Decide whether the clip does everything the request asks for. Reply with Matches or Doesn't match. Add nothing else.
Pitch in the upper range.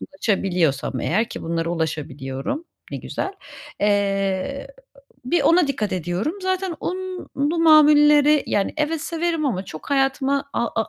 Matches